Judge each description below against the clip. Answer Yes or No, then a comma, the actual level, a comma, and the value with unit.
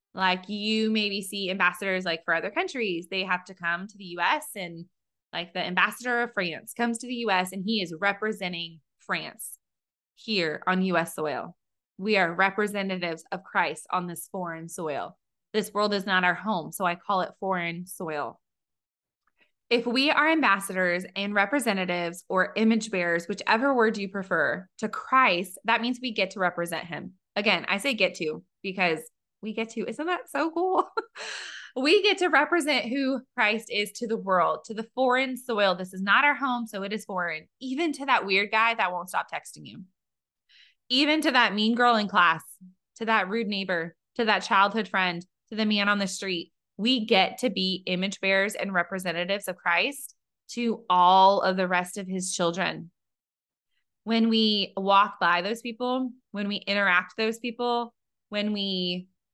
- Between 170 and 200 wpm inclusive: Yes, average, 180 wpm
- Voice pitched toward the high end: Yes, high, 200 Hz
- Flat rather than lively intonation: No, average, 3.8 semitones